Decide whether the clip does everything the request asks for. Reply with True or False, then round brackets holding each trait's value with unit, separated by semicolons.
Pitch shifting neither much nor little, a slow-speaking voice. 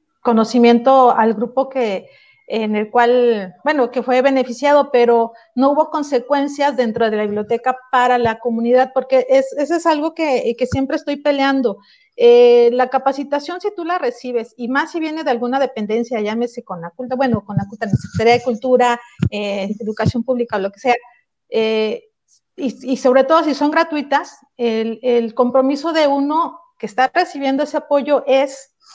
False (3.5 semitones; 170 wpm)